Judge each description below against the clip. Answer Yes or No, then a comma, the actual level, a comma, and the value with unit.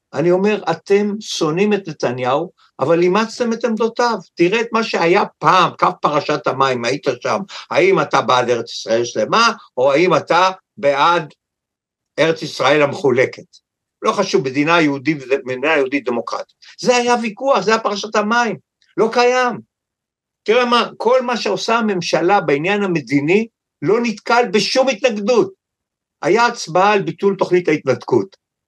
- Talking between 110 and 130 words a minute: No, average, 140 wpm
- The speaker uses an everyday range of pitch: No, wide, 7.5 semitones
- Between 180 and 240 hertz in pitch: Yes, high, 190 Hz